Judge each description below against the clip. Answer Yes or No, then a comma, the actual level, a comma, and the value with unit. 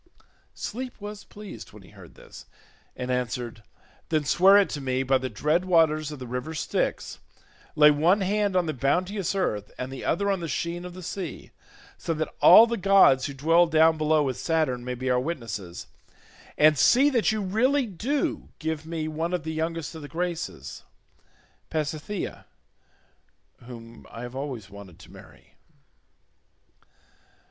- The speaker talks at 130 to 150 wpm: No, average, 165 wpm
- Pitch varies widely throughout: Yes, wide, 6.0 semitones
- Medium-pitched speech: Yes, medium, 155 Hz